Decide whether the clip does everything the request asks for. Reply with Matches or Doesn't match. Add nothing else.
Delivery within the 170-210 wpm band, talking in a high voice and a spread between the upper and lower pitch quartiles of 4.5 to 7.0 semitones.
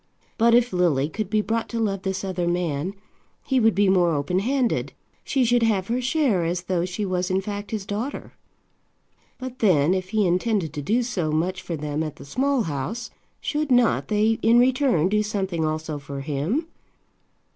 Matches